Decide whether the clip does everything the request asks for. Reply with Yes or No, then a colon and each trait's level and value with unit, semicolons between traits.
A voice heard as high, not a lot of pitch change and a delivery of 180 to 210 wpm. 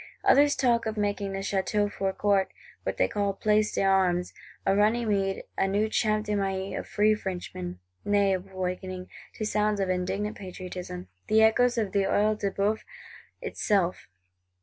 No: high, 200 Hz; narrow, 2.0 semitones; average, 155 wpm